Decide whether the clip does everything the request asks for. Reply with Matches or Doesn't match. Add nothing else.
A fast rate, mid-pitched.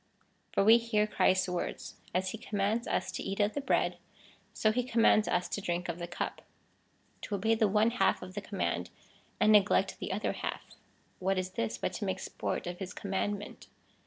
Doesn't match